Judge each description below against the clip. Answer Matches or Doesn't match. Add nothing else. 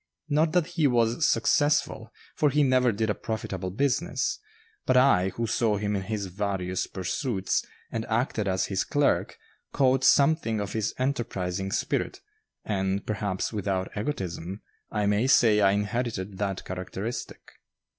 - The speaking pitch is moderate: Doesn't match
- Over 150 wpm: Doesn't match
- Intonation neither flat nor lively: Matches